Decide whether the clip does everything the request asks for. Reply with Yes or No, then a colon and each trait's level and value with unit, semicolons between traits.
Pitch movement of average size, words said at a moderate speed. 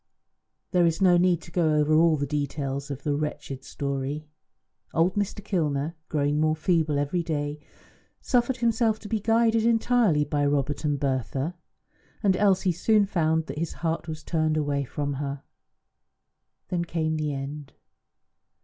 Yes: average, 3.9 semitones; average, 155 wpm